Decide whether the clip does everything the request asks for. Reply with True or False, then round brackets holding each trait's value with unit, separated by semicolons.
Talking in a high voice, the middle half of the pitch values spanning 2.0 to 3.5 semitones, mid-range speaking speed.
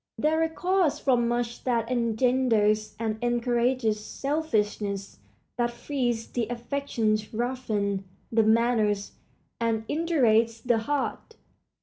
False (235 Hz; 2.8 semitones; 105 wpm)